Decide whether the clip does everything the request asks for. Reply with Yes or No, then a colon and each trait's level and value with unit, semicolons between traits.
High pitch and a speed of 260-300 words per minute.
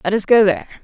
Yes: high, 210 Hz; fast, 290 wpm